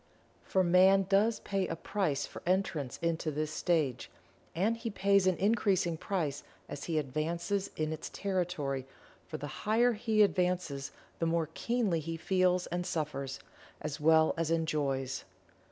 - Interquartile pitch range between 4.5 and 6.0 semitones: No, average, 4.1 semitones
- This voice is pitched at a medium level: Yes, medium, 170 Hz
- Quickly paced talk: No, average, 150 wpm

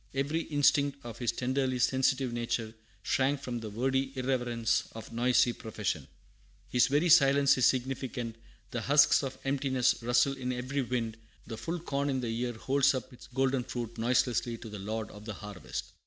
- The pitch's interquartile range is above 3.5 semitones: No, average, 2.7 semitones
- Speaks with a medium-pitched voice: No, low, 125 Hz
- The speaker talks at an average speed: Yes, average, 170 wpm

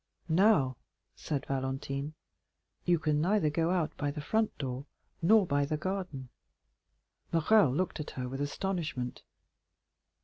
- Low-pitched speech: No, medium, 150 Hz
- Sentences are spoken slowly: Yes, slow, 130 wpm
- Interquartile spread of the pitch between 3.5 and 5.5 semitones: Yes, average, 4.7 semitones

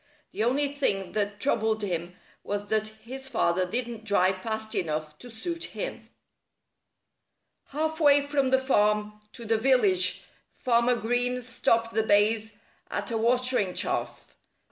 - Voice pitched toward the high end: Yes, high, 225 Hz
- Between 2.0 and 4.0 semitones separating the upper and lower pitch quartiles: Yes, average, 3.7 semitones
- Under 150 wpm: Yes, average, 140 wpm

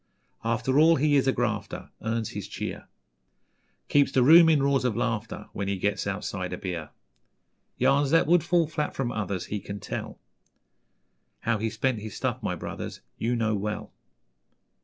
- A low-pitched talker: Yes, low, 120 Hz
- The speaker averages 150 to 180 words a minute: Yes, average, 170 wpm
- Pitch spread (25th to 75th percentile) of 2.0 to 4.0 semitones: No, average, 5.1 semitones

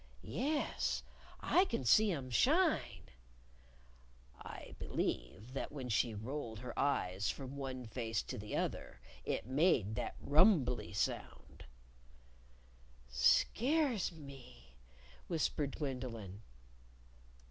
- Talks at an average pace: No, slow, 100 wpm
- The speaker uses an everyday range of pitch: No, wide, 6.5 semitones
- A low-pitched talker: Yes, low, 130 Hz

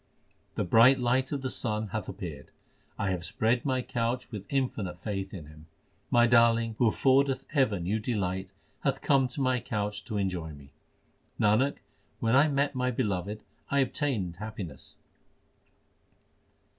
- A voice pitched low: Yes, low, 110 Hz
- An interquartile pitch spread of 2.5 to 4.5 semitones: No, average, 5.1 semitones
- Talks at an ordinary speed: Yes, average, 155 wpm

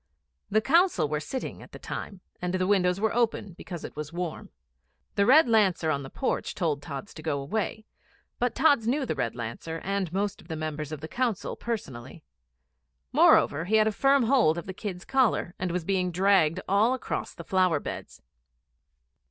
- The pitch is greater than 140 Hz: Yes, medium, 185 Hz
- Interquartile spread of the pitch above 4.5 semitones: Yes, wide, 5.6 semitones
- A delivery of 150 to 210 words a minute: Yes, average, 185 wpm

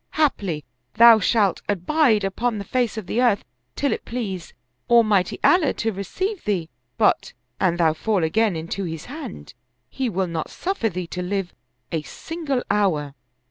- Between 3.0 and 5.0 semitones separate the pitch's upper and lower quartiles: No, wide, 5.4 semitones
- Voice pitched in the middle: No, high, 205 Hz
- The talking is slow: No, average, 160 wpm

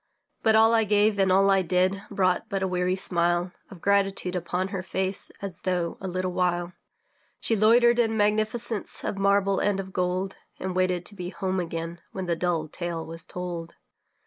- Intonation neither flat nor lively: No, narrow, 2.0 semitones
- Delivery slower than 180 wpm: No, average, 185 wpm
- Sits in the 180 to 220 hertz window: Yes, medium, 185 Hz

